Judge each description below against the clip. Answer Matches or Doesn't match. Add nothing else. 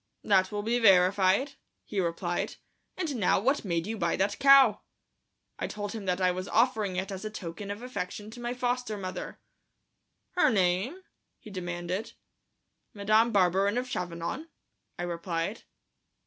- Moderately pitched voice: Doesn't match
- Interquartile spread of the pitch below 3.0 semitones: Doesn't match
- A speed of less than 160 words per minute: Matches